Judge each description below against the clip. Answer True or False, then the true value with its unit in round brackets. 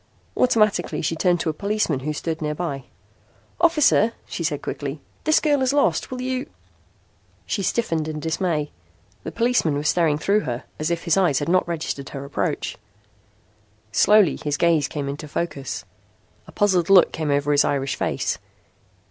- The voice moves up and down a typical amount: False (5.8 semitones)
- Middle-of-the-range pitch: True (165 Hz)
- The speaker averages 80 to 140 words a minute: False (165 wpm)